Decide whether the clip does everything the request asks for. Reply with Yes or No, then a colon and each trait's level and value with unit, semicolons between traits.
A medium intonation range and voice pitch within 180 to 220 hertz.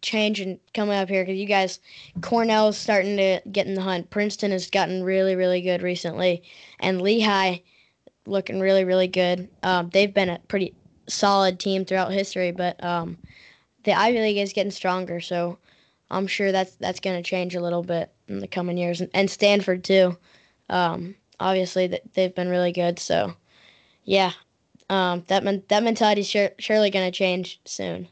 No: narrow, 1.8 semitones; high, 190 Hz